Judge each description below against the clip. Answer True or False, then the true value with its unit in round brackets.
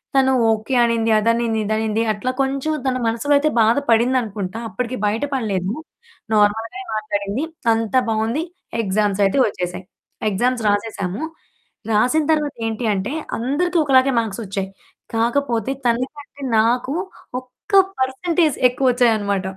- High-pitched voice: True (230 Hz)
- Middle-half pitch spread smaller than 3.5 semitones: False (3.8 semitones)